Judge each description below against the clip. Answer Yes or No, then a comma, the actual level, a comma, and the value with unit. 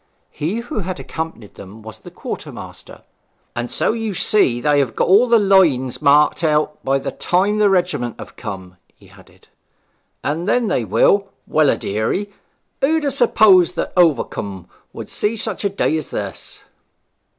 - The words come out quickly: No, average, 170 wpm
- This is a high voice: No, medium, 170 Hz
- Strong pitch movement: Yes, wide, 7.9 semitones